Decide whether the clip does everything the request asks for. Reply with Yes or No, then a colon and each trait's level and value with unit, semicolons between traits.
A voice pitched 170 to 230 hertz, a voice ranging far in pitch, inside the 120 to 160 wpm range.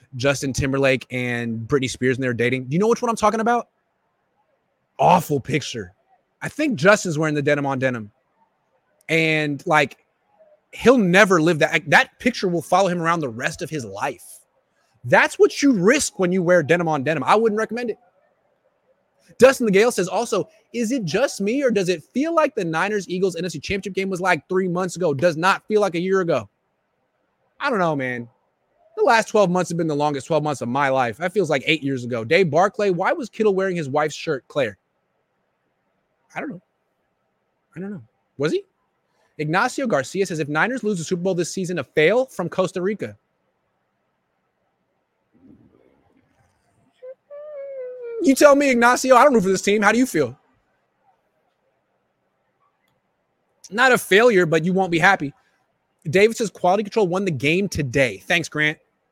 No: medium, 185 Hz; wide, 6.3 semitones; average, 180 wpm